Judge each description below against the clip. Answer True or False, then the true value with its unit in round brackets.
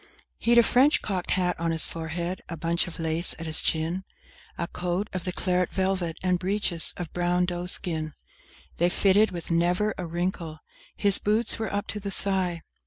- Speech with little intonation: True (2.3 semitones)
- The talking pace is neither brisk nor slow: True (190 wpm)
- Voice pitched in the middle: True (180 Hz)